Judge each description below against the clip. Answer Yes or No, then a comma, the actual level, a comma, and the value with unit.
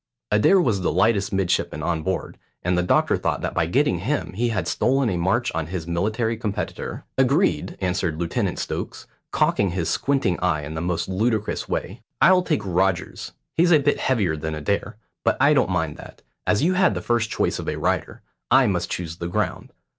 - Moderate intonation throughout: No, wide, 5.7 semitones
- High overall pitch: No, very low, 95 Hz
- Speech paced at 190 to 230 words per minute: Yes, average, 195 wpm